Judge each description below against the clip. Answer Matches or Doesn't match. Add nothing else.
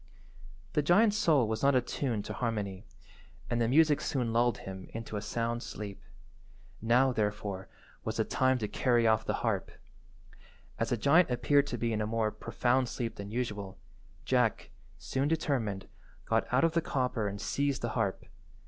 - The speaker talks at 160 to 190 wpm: Matches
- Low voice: Matches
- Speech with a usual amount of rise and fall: Matches